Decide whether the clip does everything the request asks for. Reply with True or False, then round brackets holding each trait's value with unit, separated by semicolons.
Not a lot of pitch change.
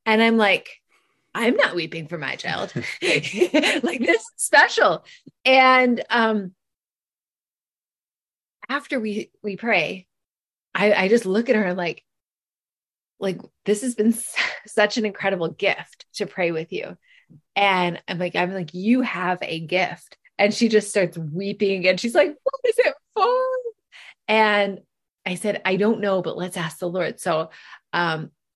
False (4.3 semitones)